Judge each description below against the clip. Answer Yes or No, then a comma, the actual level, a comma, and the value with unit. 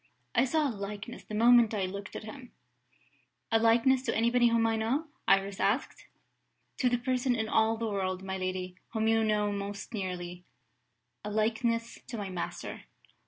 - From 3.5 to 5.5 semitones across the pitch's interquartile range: No, average, 3.1 semitones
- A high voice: Yes, high, 220 Hz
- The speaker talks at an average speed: Yes, average, 170 wpm